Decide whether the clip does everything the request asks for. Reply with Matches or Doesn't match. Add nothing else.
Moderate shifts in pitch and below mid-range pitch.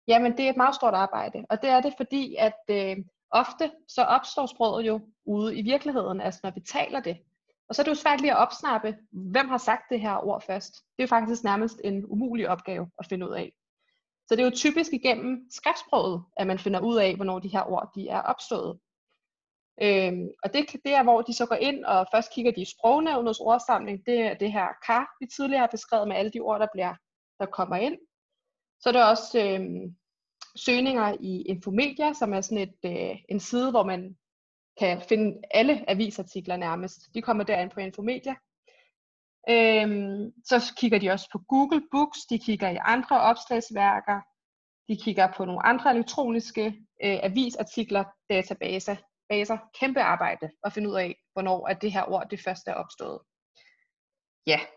Doesn't match